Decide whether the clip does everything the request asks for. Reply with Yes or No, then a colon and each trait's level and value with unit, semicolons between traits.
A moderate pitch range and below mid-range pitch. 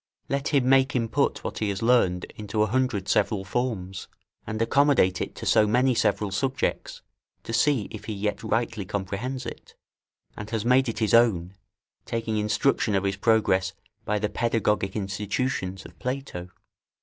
Yes: average, 4.0 semitones; low, 110 Hz